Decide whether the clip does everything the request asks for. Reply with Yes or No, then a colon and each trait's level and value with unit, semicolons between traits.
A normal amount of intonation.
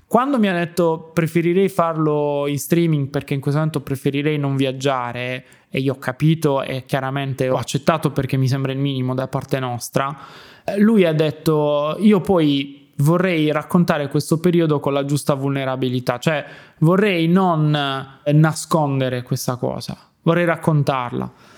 Yes: average, 3.4 semitones